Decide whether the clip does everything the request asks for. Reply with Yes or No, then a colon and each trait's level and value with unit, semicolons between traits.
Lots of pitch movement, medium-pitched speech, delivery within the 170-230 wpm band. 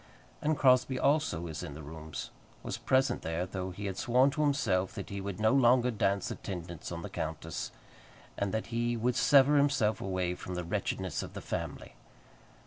No: wide, 6.4 semitones; low, 100 Hz; average, 185 wpm